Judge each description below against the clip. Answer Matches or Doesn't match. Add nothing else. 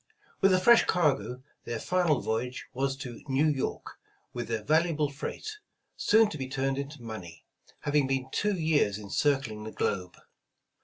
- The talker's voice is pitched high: Doesn't match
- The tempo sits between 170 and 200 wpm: Doesn't match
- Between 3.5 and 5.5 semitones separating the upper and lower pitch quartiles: Matches